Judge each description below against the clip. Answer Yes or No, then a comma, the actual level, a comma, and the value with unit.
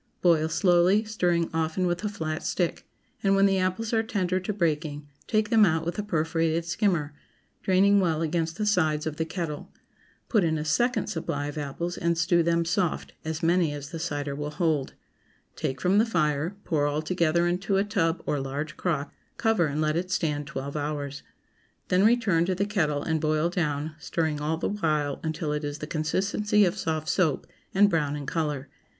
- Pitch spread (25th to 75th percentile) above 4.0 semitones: No, average, 3.5 semitones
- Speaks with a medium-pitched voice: Yes, medium, 165 Hz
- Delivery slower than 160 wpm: No, average, 190 wpm